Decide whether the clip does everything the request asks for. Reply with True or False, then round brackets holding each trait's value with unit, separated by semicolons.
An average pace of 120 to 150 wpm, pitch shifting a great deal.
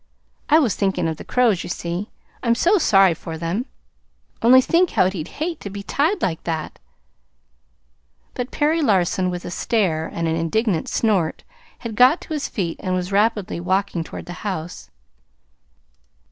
False (170 wpm; 6.1 semitones)